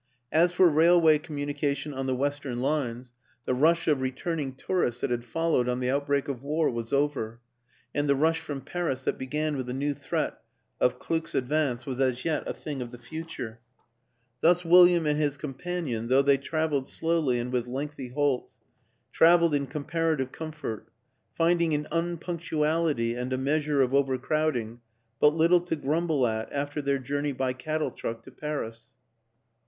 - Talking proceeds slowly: No, average, 170 wpm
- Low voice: No, medium, 145 Hz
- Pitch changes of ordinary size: Yes, average, 3.7 semitones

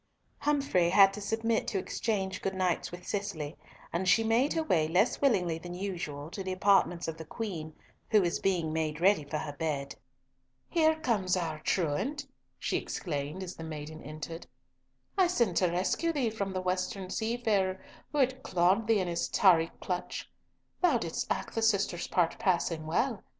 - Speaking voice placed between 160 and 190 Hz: Yes, medium, 185 Hz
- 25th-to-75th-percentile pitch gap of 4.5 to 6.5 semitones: Yes, average, 5.0 semitones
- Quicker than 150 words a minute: Yes, average, 175 wpm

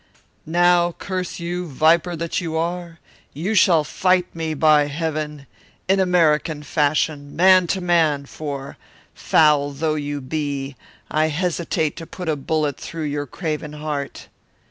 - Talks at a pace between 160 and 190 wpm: No, average, 140 wpm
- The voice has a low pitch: No, medium, 155 Hz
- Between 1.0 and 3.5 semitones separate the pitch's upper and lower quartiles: Yes, average, 2.8 semitones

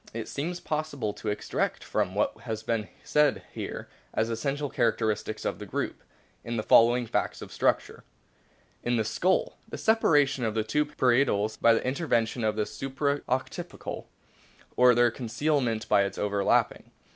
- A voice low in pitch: Yes, low, 120 Hz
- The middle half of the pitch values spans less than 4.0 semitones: No, average, 4.3 semitones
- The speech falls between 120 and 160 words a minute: Yes, average, 155 wpm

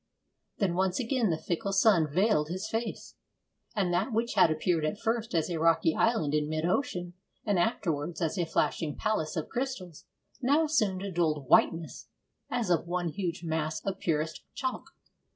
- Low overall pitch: No, medium, 175 Hz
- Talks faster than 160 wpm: Yes, average, 170 wpm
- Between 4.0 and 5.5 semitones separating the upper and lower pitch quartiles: Yes, average, 5.1 semitones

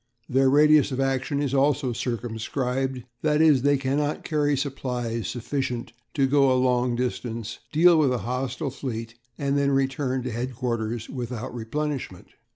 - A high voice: No, low, 130 Hz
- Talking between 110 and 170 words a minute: Yes, average, 150 wpm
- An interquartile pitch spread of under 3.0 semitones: Yes, narrow, 2.6 semitones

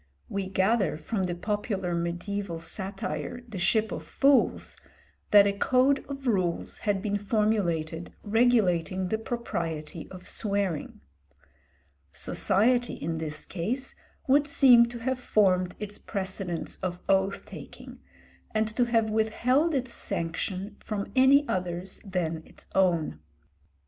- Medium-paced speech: No, slow, 125 wpm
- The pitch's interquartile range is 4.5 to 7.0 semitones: Yes, average, 4.8 semitones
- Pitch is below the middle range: No, high, 200 Hz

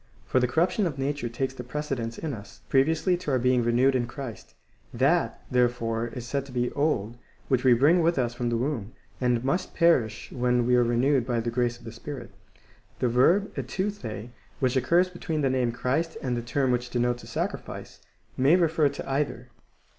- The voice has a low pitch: Yes, low, 125 Hz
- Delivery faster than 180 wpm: Yes, average, 200 wpm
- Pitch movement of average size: Yes, average, 3.3 semitones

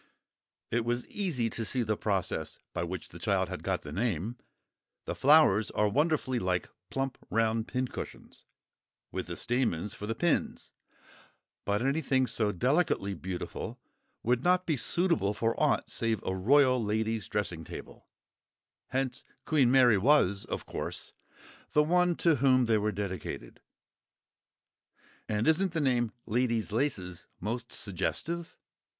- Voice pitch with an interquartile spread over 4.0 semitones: Yes, average, 4.9 semitones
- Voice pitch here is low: Yes, low, 120 Hz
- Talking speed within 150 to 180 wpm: No, slow, 135 wpm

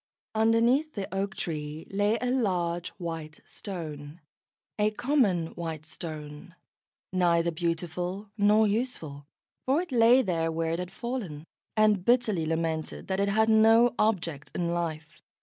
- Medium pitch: Yes, medium, 180 Hz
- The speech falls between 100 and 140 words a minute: Yes, slow, 135 wpm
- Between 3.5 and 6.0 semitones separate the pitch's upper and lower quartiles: Yes, average, 5.1 semitones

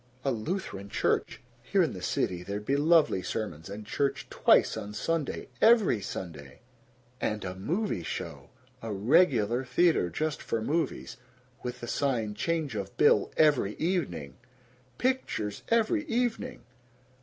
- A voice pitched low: Yes, low, 125 Hz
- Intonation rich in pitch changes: Yes, wide, 8.6 semitones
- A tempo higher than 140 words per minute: No, slow, 135 wpm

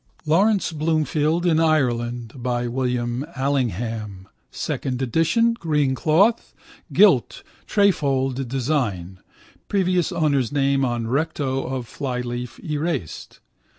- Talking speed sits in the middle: No, slow, 95 wpm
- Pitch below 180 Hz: Yes, low, 135 Hz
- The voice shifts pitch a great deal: No, average, 4.5 semitones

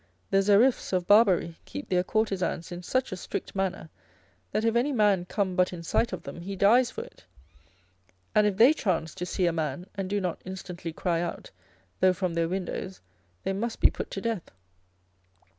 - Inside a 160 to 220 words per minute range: Yes, average, 195 wpm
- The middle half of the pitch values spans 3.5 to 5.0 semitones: No, average, 2.9 semitones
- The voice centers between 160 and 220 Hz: Yes, high, 190 Hz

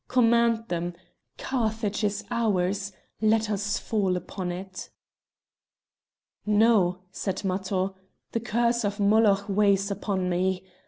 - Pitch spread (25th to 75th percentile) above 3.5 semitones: No, average, 2.8 semitones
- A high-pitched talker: Yes, high, 205 Hz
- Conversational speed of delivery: No, slow, 110 wpm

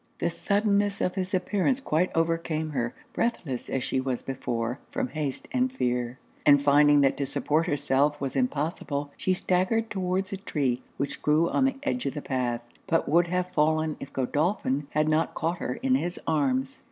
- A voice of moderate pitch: Yes, medium, 155 Hz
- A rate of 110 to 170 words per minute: No, average, 180 wpm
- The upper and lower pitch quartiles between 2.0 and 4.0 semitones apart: No, average, 5.0 semitones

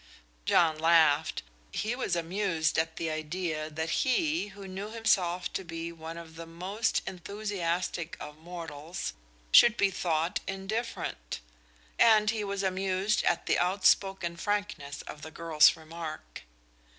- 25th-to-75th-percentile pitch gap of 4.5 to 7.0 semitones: No, average, 3.7 semitones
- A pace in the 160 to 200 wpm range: No, slow, 135 wpm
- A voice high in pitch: No, medium, 175 Hz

